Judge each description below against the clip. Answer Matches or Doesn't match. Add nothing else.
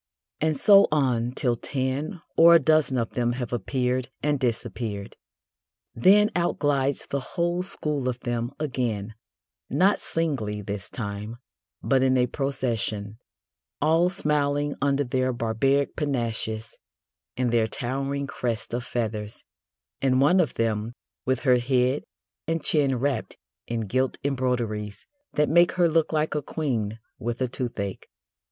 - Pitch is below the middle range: Matches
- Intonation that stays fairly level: Doesn't match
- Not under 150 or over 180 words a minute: Doesn't match